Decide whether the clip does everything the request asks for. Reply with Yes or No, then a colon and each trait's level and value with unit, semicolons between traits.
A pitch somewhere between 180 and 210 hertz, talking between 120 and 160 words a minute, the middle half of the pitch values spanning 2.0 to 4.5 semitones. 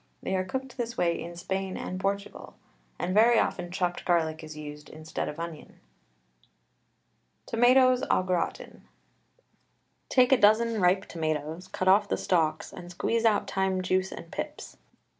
Yes: medium, 185 Hz; average, 150 wpm; average, 4.0 semitones